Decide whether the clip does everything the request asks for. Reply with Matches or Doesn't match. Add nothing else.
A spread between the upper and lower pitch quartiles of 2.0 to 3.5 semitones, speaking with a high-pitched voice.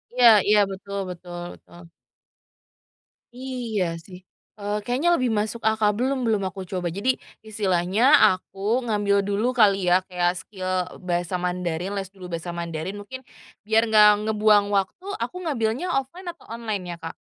Doesn't match